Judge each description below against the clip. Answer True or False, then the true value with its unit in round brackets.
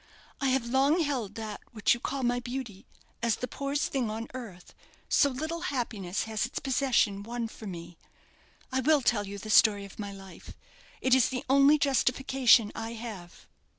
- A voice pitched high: True (240 Hz)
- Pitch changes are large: False (4.3 semitones)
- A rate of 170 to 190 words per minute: True (180 wpm)